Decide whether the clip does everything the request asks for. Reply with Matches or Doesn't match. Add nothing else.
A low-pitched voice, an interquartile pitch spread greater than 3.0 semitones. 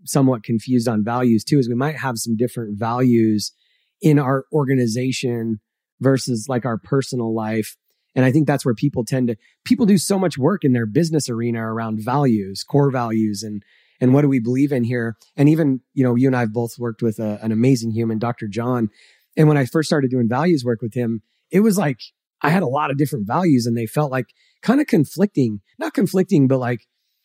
Matches